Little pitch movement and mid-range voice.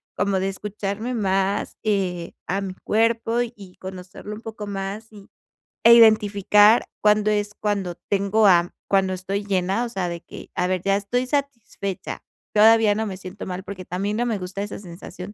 No: narrow, 2.3 semitones; high, 200 Hz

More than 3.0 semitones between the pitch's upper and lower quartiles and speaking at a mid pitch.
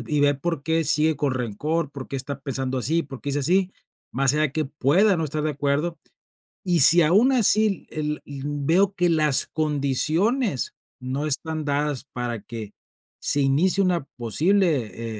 Yes: average, 3.7 semitones; medium, 150 Hz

